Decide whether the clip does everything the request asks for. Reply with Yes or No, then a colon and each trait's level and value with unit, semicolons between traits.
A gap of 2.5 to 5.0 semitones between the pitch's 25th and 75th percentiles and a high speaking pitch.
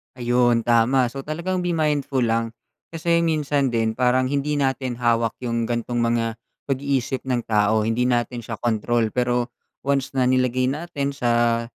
No: average, 2.8 semitones; low, 125 Hz